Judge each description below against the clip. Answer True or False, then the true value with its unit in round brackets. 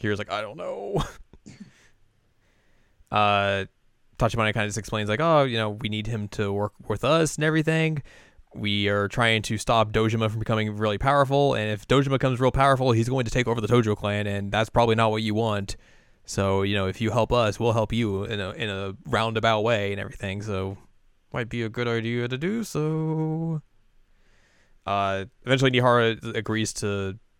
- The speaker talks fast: False (190 wpm)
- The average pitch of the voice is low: True (110 Hz)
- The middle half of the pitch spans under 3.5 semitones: True (2.9 semitones)